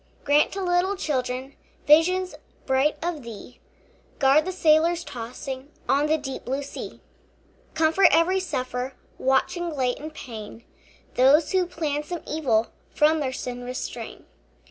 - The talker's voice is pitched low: No, very high, 295 Hz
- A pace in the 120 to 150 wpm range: Yes, slow, 135 wpm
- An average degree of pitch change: Yes, average, 4.3 semitones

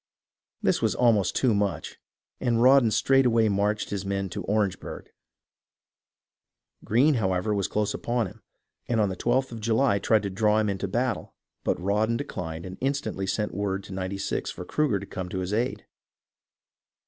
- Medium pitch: No, low, 105 Hz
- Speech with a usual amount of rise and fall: Yes, average, 3.3 semitones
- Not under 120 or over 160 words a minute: No, average, 175 wpm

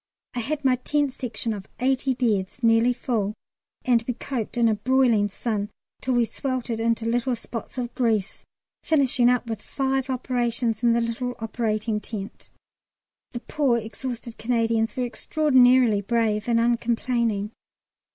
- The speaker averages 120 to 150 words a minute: Yes, average, 145 wpm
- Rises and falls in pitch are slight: Yes, narrow, 2.1 semitones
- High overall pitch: Yes, high, 235 Hz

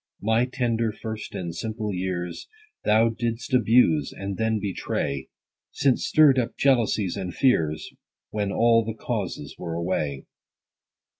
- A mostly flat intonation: No, average, 4.2 semitones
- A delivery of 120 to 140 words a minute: Yes, slow, 135 wpm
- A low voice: Yes, low, 110 Hz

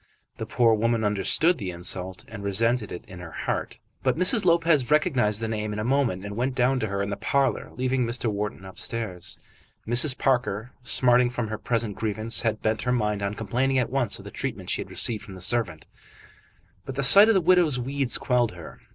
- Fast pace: Yes, fast, 210 wpm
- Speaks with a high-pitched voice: No, low, 115 Hz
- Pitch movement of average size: Yes, average, 4.0 semitones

